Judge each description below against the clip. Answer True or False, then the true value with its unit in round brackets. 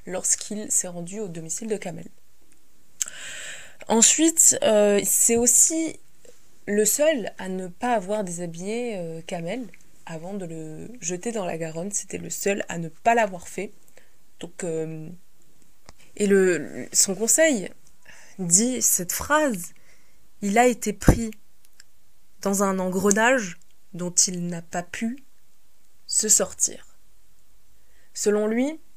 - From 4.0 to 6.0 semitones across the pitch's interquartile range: True (4.6 semitones)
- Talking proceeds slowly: True (125 wpm)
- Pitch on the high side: True (205 Hz)